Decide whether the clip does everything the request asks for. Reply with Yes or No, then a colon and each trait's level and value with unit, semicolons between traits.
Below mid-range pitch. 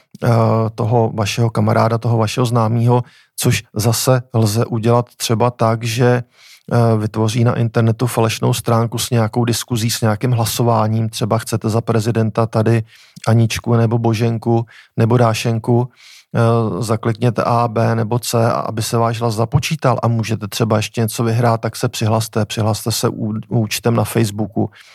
Yes: low, 115 Hz